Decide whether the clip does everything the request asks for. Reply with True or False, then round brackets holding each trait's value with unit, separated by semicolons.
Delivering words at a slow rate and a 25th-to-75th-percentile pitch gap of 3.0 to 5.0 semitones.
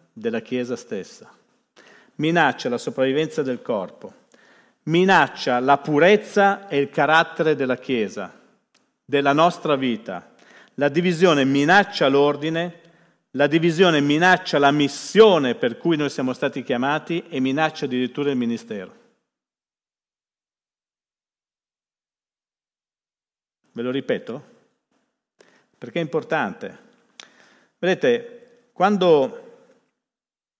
True (90 wpm; 4.2 semitones)